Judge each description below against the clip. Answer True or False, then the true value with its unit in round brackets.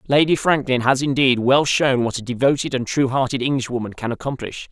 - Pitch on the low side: True (130 Hz)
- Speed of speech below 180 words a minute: False (205 wpm)